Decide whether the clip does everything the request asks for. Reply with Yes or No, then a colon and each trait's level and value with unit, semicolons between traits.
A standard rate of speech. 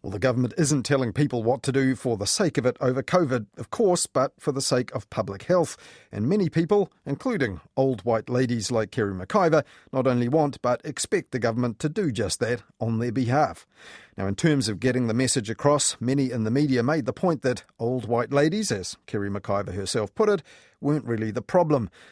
No: fast, 210 wpm